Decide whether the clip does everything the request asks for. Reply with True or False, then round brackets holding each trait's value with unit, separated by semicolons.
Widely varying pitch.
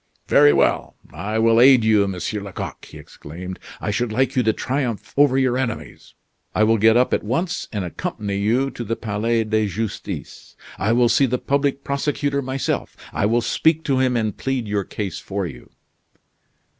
False (4.1 semitones)